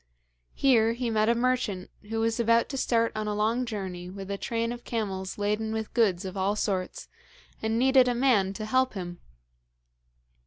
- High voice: Yes, high, 220 Hz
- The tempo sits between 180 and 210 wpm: Yes, average, 185 wpm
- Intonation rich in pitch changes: No, average, 3.0 semitones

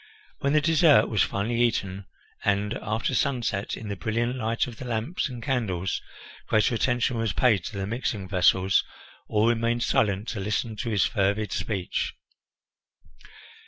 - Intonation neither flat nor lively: Yes, average, 3.2 semitones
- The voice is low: Yes, low, 110 Hz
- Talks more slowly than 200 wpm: Yes, average, 155 wpm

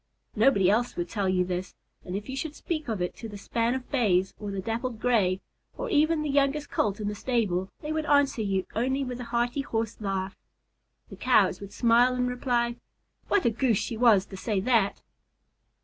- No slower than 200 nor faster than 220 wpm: Yes, fast, 205 wpm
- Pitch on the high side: Yes, high, 230 Hz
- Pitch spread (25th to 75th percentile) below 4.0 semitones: No, average, 4.6 semitones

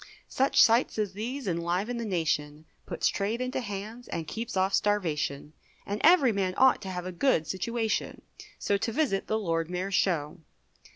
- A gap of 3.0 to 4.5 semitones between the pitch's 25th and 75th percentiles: No, average, 4.9 semitones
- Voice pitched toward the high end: Yes, high, 200 Hz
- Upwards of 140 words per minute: Yes, average, 170 wpm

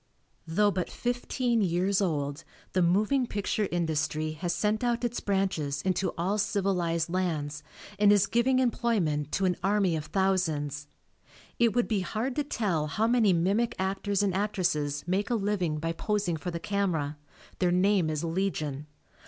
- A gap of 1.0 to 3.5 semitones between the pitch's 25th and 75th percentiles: No, average, 4.4 semitones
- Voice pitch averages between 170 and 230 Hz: Yes, high, 190 Hz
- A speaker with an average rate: Yes, average, 160 wpm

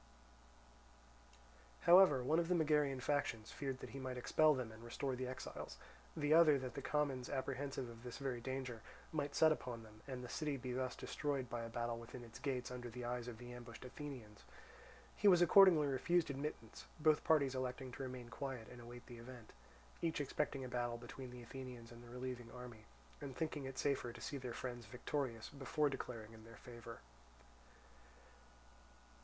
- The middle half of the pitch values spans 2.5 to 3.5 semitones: Yes, average, 3.0 semitones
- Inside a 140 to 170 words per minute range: No, average, 185 wpm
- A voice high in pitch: No, low, 130 Hz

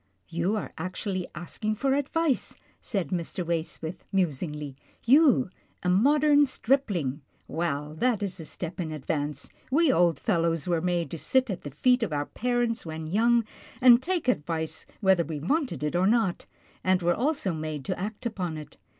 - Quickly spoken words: No, average, 175 wpm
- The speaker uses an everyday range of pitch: No, wide, 6.9 semitones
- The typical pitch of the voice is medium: Yes, medium, 180 Hz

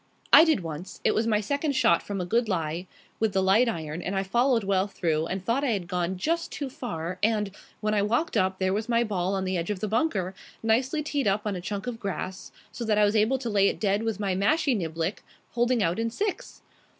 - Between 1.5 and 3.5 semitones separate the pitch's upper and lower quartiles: No, average, 3.9 semitones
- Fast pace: Yes, fast, 245 wpm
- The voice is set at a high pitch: Yes, high, 210 Hz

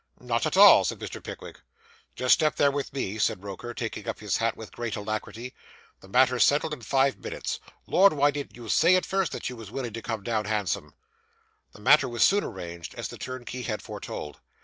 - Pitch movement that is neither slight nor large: Yes, average, 4.4 semitones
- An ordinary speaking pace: No, fast, 210 wpm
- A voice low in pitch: Yes, low, 120 Hz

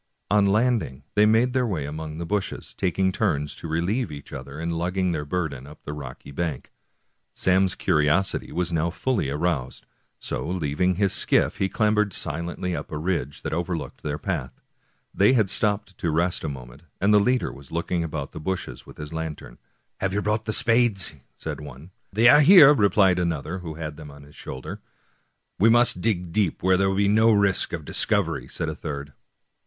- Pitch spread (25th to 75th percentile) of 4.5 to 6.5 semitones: Yes, average, 5.1 semitones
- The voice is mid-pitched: No, very low, 90 Hz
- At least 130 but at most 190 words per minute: No, fast, 205 wpm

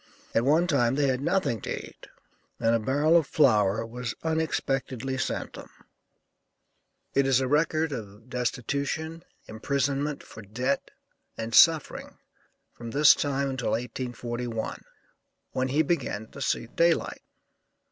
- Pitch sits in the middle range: No, low, 130 Hz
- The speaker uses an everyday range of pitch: Yes, average, 3.9 semitones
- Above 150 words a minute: No, slow, 135 wpm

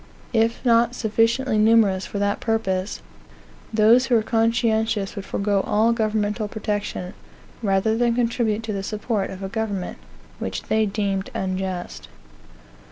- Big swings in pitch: No, narrow, 2.4 semitones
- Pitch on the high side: Yes, high, 215 Hz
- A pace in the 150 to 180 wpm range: No, slow, 135 wpm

